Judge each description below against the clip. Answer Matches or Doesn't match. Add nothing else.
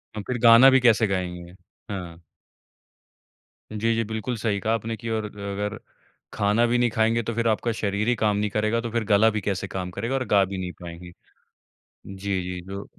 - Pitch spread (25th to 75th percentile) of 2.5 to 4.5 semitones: Matches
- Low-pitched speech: Matches